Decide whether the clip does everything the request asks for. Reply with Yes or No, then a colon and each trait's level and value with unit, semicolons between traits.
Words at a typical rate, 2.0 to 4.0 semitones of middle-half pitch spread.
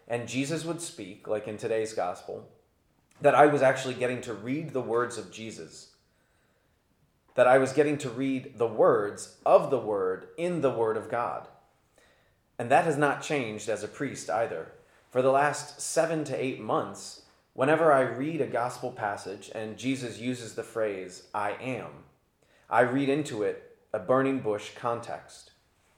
No: average, 165 wpm; average, 4.5 semitones